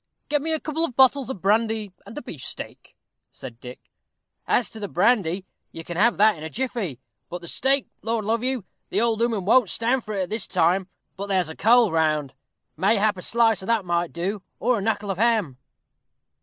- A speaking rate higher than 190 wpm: Yes, fast, 205 wpm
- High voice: Yes, high, 210 Hz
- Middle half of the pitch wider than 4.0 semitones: Yes, average, 4.7 semitones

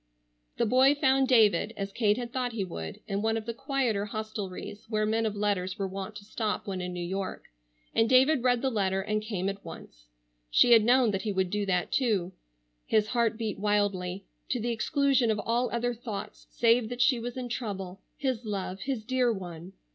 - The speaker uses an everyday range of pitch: Yes, average, 3.7 semitones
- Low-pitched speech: No, high, 215 Hz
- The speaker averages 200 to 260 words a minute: Yes, fast, 205 wpm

